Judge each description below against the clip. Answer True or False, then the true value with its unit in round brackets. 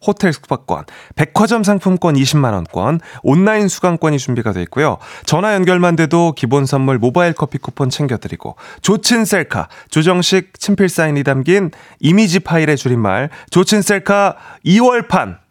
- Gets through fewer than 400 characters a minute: True (310 characters per minute)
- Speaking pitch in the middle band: True (165 Hz)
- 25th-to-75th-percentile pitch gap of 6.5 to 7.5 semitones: False (6.0 semitones)